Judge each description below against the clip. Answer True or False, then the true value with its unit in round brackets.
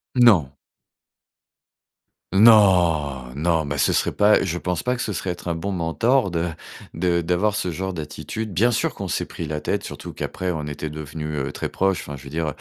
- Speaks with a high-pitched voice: False (85 Hz)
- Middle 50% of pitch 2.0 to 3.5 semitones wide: False (4.2 semitones)